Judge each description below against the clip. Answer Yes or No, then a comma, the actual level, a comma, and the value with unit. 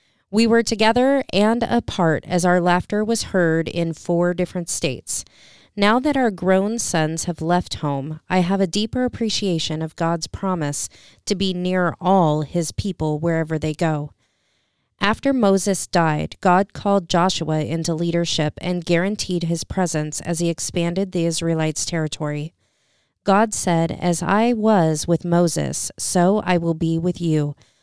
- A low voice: No, medium, 175 Hz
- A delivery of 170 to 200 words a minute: No, average, 150 wpm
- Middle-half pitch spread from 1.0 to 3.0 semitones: No, average, 3.5 semitones